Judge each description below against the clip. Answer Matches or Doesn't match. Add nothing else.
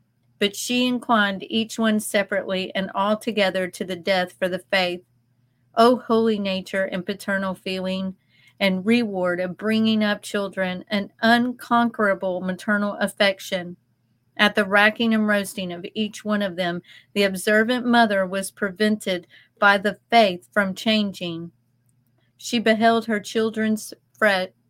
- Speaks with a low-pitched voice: Doesn't match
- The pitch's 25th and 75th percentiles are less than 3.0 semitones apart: Matches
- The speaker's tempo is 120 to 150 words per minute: Matches